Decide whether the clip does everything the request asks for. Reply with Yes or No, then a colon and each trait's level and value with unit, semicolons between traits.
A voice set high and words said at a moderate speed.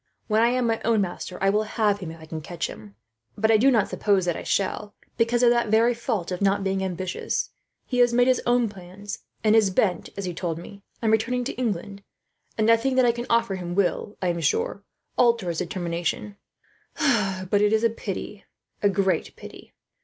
No: high, 205 Hz; fast, 215 wpm